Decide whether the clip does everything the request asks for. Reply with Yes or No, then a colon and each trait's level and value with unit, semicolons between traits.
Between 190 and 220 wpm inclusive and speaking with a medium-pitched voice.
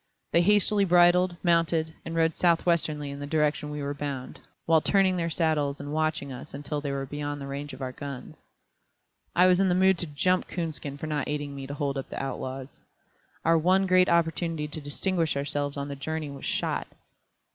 Yes: average, 200 wpm; medium, 155 Hz